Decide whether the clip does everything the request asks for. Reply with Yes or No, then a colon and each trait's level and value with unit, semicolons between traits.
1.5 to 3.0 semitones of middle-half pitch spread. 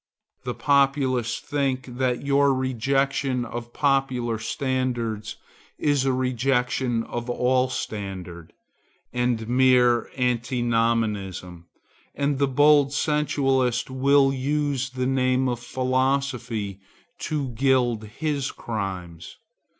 Yes: narrow, 2.5 semitones